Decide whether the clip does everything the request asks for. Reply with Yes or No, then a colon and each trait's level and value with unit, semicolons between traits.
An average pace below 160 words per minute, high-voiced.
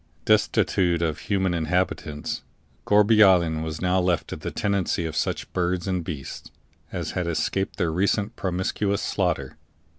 No: average, 145 wpm; very low, 90 Hz